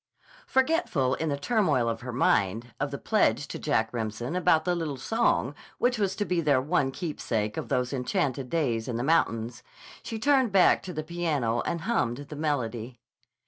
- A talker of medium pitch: Yes, medium, 145 Hz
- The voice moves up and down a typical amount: No, wide, 6.5 semitones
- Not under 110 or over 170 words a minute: No, average, 185 wpm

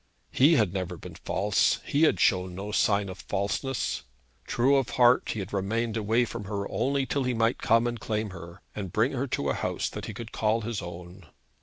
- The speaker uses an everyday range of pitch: Yes, average, 3.8 semitones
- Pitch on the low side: Yes, low, 110 Hz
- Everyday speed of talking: No, fast, 210 wpm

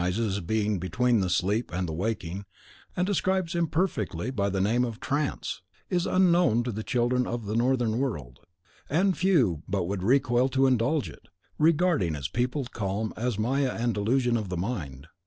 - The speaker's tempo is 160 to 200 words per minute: Yes, average, 180 wpm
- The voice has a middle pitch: No, low, 115 Hz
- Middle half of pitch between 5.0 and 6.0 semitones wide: Yes, wide, 5.4 semitones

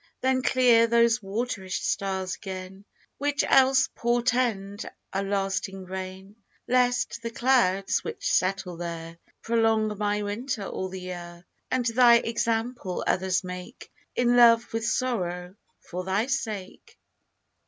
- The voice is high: Yes, high, 210 Hz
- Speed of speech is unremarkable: No, slow, 120 wpm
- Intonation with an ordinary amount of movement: Yes, average, 4.1 semitones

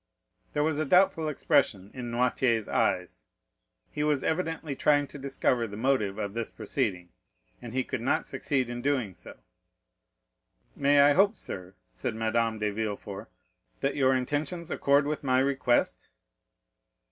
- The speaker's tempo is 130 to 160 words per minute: Yes, average, 145 wpm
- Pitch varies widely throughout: No, average, 4.6 semitones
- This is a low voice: Yes, low, 130 Hz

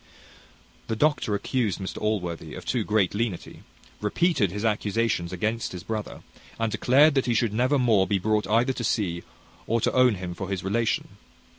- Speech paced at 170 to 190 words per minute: Yes, average, 175 wpm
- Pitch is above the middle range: No, low, 110 Hz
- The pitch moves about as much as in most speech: Yes, average, 3.4 semitones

